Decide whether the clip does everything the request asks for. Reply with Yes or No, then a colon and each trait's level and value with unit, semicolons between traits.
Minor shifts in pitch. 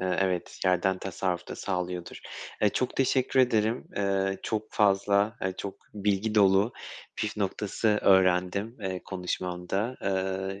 Yes: narrow, 2.2 semitones